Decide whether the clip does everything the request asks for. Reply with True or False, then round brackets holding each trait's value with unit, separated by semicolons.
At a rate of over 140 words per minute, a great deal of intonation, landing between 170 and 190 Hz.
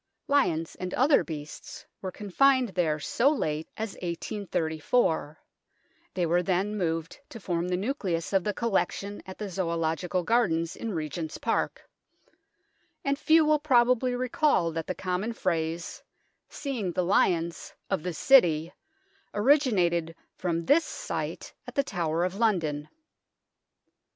False (135 wpm; 5.9 semitones; 185 Hz)